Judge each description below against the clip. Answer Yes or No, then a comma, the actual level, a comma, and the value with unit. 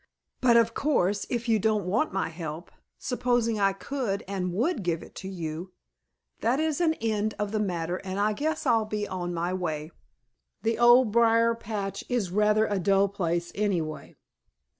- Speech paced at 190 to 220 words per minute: No, average, 175 wpm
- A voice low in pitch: No, high, 205 Hz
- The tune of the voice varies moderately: Yes, average, 4.1 semitones